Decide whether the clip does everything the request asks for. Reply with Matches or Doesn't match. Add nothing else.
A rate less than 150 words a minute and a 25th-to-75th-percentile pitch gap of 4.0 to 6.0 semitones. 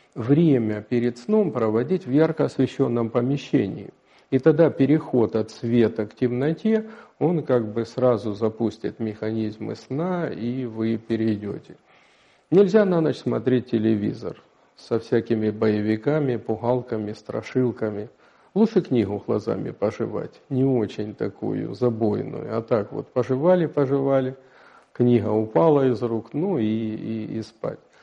Matches